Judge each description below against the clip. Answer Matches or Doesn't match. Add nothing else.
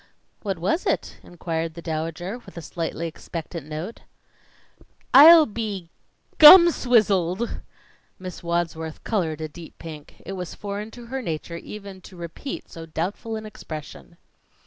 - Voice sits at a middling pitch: Matches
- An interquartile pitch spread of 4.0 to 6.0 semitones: Matches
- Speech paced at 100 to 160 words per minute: Matches